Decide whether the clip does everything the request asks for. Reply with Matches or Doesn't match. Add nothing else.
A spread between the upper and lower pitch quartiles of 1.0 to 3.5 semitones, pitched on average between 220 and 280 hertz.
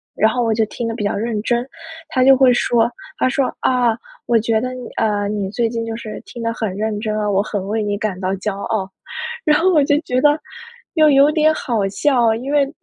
Matches